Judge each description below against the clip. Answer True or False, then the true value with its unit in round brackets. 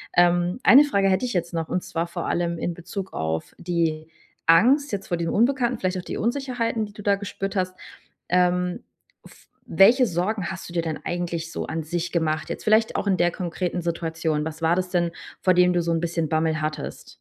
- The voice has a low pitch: False (175 Hz)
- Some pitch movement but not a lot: True (3.0 semitones)